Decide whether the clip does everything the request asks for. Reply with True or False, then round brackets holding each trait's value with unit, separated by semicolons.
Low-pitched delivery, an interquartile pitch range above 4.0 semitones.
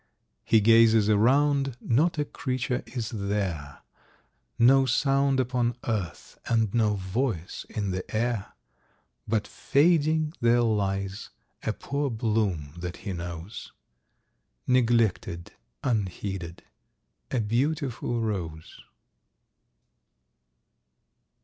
True (115 Hz; 4.8 semitones)